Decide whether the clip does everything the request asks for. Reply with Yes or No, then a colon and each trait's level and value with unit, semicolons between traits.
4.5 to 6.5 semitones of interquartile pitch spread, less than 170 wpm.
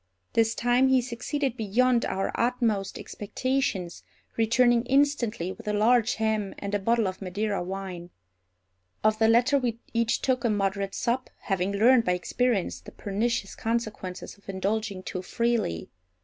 No: average, 3.7 semitones; average, 150 wpm